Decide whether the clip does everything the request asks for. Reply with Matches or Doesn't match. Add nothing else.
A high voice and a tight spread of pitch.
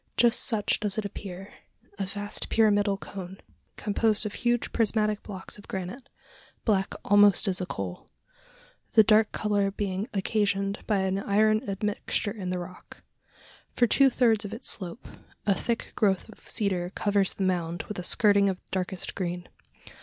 Matches